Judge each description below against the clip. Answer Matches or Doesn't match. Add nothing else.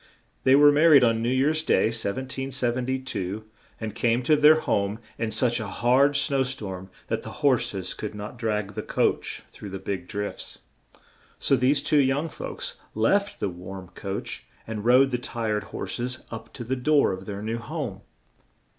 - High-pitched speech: Doesn't match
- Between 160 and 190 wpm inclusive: Matches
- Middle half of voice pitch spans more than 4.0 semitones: Matches